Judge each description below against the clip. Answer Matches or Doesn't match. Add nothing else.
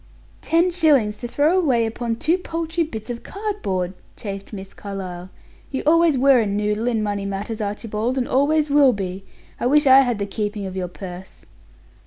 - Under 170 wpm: Doesn't match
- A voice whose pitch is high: Matches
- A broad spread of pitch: Matches